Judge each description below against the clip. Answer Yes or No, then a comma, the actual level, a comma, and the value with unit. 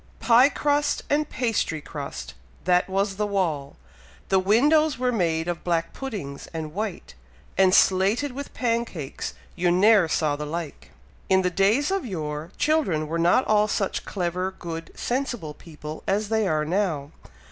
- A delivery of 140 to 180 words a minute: Yes, average, 155 wpm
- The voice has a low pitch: No, high, 190 Hz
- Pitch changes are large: Yes, wide, 5.9 semitones